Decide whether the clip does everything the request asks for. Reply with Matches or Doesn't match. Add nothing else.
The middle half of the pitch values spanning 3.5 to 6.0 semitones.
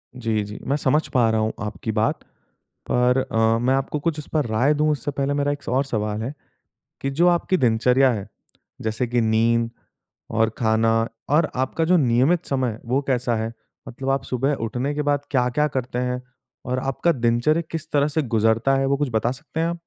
Matches